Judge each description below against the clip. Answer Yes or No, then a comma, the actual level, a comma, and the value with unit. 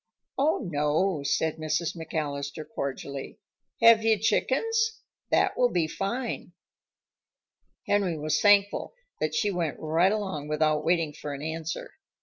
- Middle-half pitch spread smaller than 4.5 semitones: No, average, 5.2 semitones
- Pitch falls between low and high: Yes, medium, 165 Hz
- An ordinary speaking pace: No, slow, 130 wpm